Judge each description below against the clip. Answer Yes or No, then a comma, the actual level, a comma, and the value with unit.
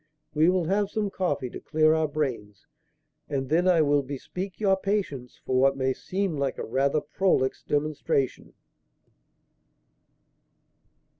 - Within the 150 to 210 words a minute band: No, slow, 135 wpm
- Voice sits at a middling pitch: Yes, medium, 150 Hz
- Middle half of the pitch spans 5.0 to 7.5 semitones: Yes, average, 5.3 semitones